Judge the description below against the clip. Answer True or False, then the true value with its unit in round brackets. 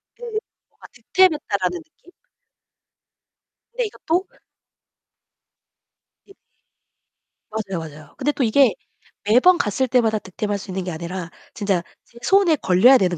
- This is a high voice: True (220 Hz)